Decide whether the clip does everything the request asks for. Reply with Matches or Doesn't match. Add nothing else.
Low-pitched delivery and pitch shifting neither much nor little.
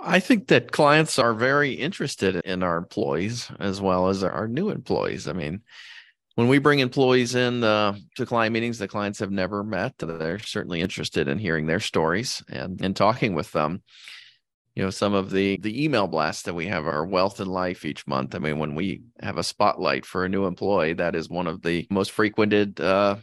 Matches